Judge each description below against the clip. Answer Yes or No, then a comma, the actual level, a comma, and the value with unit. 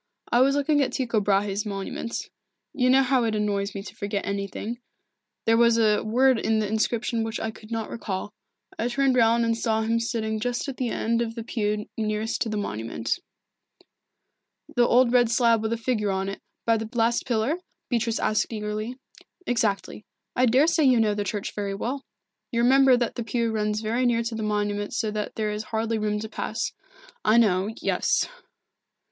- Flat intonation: Yes, narrow, 2.2 semitones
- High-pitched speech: Yes, high, 225 Hz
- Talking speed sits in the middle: Yes, average, 190 wpm